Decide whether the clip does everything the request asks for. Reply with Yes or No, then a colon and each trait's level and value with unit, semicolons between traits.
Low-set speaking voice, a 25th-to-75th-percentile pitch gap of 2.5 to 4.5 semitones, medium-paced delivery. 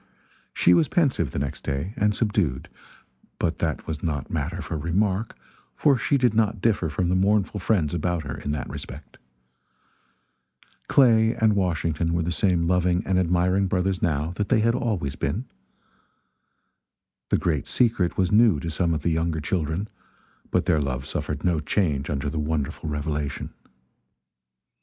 No: very low, 85 Hz; average, 5.1 semitones; average, 160 wpm